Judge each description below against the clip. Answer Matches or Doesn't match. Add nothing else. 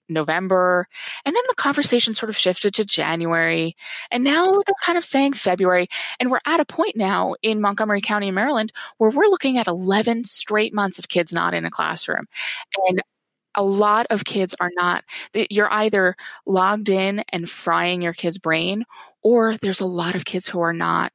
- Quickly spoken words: Doesn't match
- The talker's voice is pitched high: Matches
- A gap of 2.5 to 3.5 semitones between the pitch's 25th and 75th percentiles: Doesn't match